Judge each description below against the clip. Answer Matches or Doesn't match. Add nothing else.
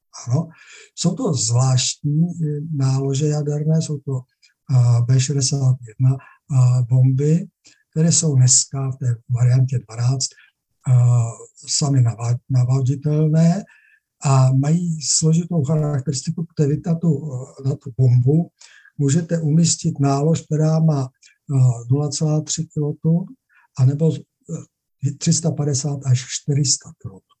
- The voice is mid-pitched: Matches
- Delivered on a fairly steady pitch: Doesn't match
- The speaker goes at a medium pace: Doesn't match